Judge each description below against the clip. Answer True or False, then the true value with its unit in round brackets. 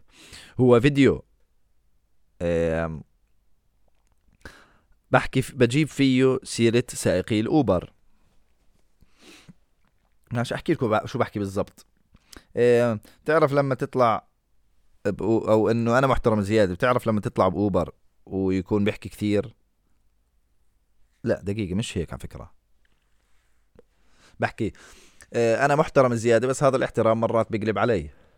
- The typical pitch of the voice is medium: False (110 Hz)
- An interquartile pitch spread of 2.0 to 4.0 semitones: False (4.5 semitones)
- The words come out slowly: True (95 wpm)